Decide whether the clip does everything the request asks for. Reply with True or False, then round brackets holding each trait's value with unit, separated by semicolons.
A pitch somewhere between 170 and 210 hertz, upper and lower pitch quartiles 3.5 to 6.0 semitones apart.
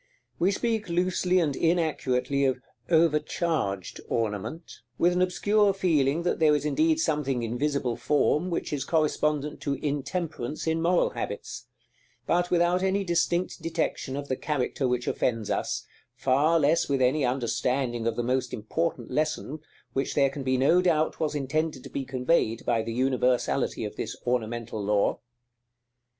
False (145 Hz; 5.0 semitones)